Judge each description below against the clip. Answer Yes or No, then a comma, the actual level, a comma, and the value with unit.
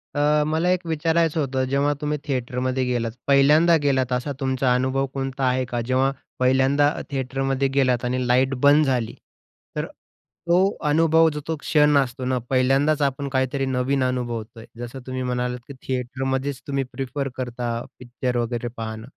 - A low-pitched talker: Yes, low, 130 Hz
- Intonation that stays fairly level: Yes, narrow, 2.2 semitones